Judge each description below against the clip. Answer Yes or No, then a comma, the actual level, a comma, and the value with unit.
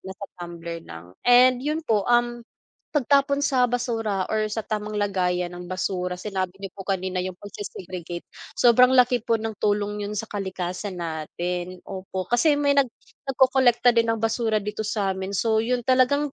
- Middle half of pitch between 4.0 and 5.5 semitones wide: Yes, average, 4.6 semitones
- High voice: Yes, high, 210 Hz